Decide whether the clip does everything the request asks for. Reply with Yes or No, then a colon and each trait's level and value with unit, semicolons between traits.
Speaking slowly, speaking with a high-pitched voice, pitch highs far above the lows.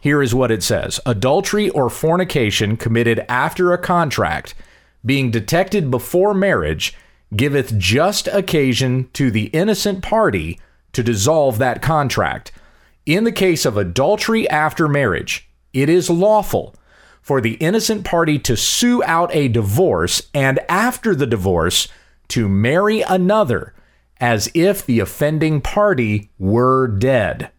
No: slow, 130 wpm; medium, 140 Hz; wide, 7.8 semitones